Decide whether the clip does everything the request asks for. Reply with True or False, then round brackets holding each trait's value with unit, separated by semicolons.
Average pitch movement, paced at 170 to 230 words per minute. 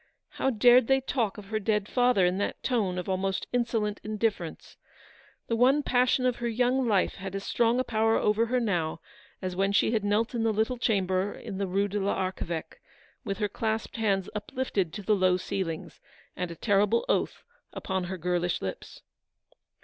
True (3.6 semitones; 185 wpm)